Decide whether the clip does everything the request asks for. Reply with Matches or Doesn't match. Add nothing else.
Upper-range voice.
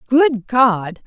Matches